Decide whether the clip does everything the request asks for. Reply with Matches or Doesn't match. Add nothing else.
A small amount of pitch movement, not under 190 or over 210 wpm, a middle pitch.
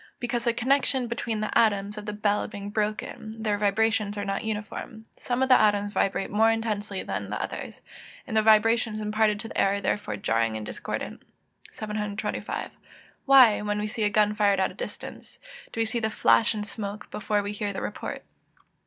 Doesn't match